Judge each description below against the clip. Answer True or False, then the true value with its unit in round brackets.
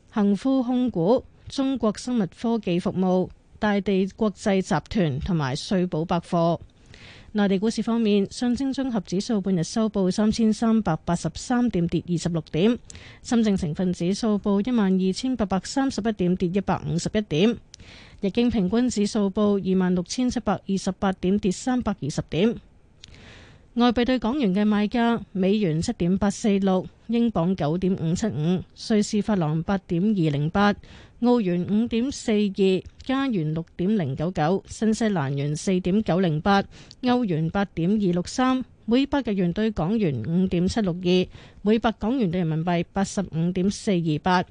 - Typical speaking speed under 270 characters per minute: True (250 characters per minute)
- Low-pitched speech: False (200 Hz)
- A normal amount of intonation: True (3.8 semitones)